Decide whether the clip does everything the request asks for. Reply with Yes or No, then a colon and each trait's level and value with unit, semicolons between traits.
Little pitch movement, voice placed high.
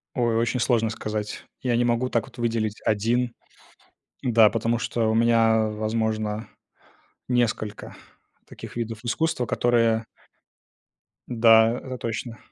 No: narrow, 1.5 semitones; low, 115 Hz